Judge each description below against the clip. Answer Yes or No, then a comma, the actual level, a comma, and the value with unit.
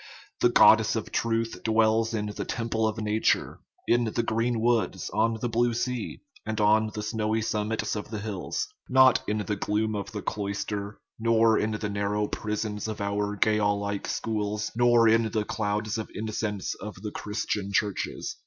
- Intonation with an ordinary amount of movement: No, narrow, 1.5 semitones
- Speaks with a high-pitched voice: No, low, 110 Hz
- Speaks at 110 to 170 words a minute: No, average, 180 wpm